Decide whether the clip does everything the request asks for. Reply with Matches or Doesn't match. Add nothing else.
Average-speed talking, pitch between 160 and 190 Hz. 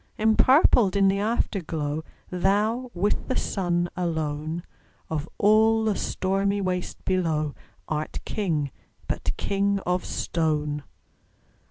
Doesn't match